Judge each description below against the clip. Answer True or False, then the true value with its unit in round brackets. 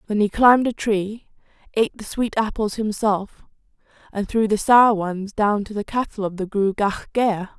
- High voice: True (210 Hz)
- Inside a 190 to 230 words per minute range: False (180 wpm)